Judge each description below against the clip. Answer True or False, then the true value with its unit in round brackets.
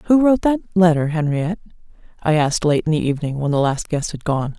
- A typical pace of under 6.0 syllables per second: False (6.4 syllables/s)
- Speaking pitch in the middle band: True (165 Hz)